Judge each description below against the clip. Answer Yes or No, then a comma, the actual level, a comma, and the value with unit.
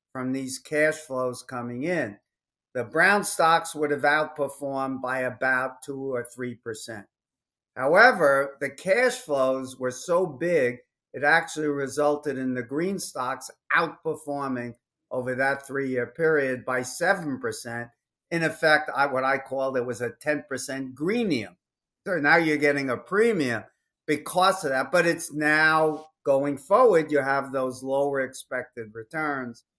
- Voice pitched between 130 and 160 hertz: Yes, medium, 140 Hz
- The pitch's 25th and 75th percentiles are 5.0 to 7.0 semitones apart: No, average, 3.0 semitones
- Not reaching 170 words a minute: Yes, average, 140 wpm